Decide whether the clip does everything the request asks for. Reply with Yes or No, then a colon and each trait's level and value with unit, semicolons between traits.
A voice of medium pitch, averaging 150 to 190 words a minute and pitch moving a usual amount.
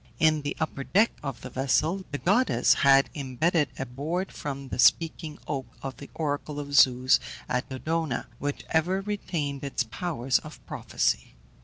Yes: medium, 145 Hz; average, 160 wpm; average, 3.4 semitones